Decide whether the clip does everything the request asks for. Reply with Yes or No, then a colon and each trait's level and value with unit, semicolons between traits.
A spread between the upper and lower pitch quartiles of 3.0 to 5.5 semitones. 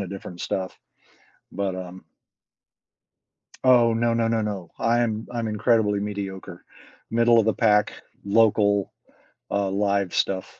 No: narrow, 2.6 semitones